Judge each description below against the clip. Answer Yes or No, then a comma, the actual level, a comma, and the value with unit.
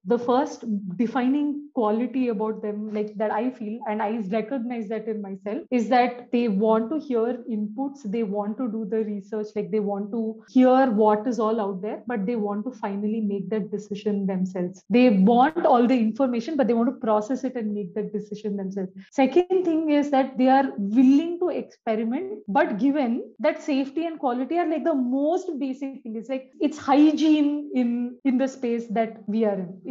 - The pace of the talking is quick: No, average, 195 wpm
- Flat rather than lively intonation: No, average, 4.0 semitones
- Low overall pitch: No, high, 235 Hz